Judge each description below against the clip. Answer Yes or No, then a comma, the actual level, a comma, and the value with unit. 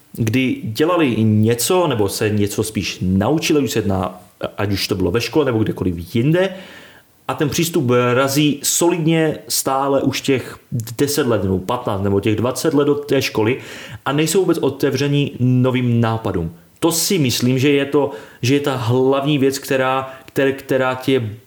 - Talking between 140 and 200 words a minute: Yes, average, 160 wpm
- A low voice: Yes, low, 130 Hz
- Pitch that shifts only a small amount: No, average, 4.7 semitones